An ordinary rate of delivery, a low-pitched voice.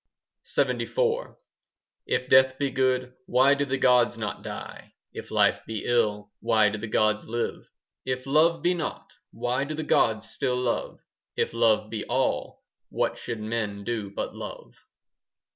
Yes: average, 160 wpm; low, 120 Hz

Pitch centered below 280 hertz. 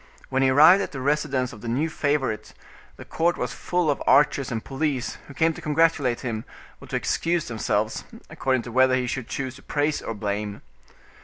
Yes: low, 135 Hz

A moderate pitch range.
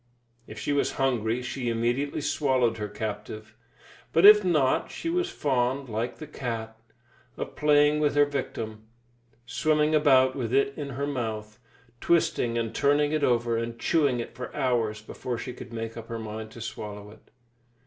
Yes: average, 4.3 semitones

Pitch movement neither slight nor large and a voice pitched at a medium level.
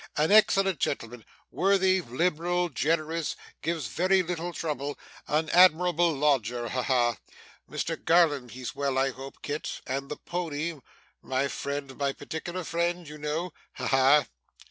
Yes: average, 4.1 semitones; medium, 150 Hz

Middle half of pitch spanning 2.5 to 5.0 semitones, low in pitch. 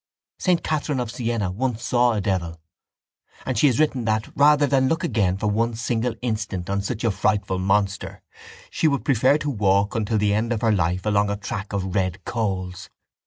Yes: average, 3.9 semitones; low, 110 Hz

